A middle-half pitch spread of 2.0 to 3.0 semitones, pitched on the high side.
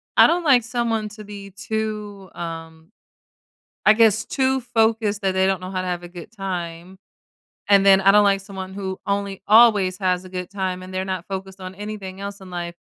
Yes: narrow, 2.4 semitones; high, 195 Hz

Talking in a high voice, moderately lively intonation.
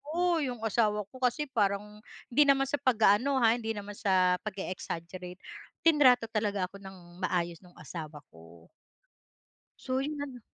No: high, 210 Hz; wide, 5.9 semitones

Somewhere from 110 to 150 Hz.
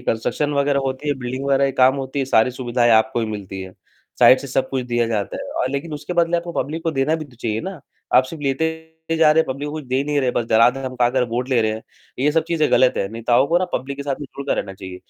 Yes: low, 135 Hz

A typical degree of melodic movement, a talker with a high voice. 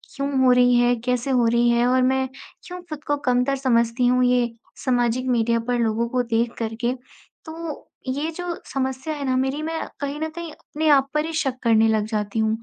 Yes: average, 3.2 semitones; very high, 255 Hz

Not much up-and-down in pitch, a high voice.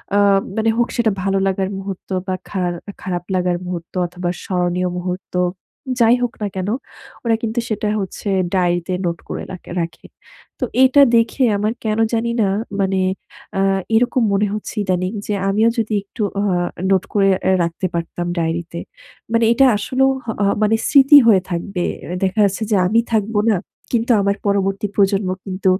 No: average, 3.5 semitones; high, 195 Hz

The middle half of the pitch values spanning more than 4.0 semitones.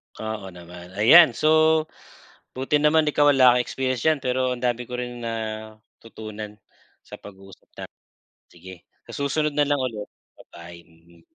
Yes: wide, 5.6 semitones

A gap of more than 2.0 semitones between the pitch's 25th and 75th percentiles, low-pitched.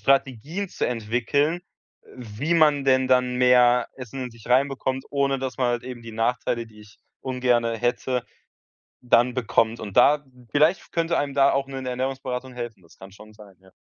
Yes: average, 2.7 semitones; low, 125 Hz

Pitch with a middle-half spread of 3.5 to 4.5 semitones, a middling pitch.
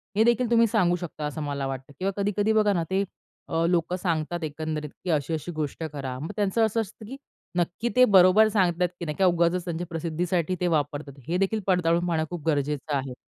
Yes: average, 3.9 semitones; medium, 175 Hz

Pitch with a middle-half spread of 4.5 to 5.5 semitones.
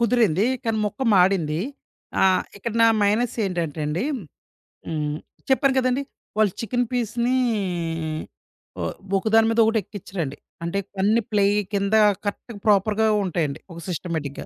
Yes: average, 4.8 semitones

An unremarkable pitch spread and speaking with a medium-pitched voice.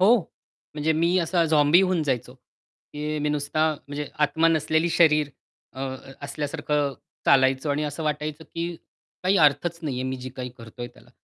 No: narrow, 2.3 semitones; medium, 150 Hz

